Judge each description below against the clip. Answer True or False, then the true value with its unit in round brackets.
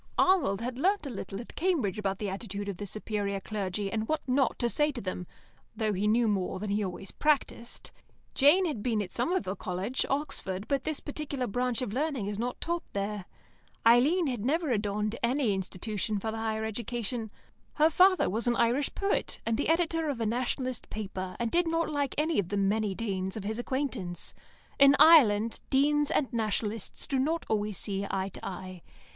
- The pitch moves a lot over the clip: True (5.7 semitones)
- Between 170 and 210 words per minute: True (190 wpm)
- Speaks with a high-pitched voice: True (230 Hz)